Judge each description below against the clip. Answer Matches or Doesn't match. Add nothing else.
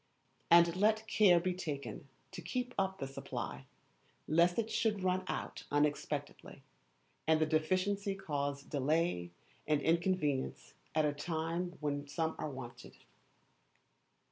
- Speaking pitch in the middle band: Matches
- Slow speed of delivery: Matches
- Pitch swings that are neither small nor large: Matches